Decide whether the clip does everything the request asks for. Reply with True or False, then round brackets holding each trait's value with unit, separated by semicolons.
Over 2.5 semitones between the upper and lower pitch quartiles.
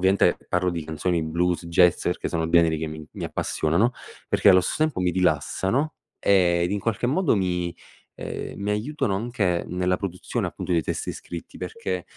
True (2.9 semitones)